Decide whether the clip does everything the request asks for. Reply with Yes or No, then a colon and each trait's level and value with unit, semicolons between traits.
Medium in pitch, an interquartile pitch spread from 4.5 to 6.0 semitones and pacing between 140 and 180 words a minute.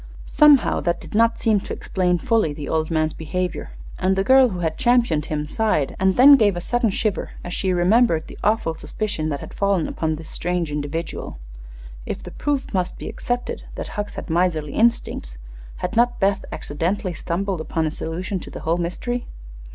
No: medium, 180 Hz; wide, 5.5 semitones; average, 190 wpm